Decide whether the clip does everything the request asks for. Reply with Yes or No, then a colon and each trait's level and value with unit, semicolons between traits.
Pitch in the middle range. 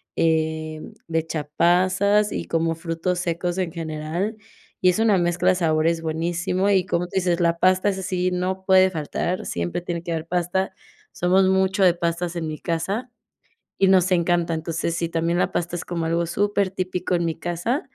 Yes: medium, 175 Hz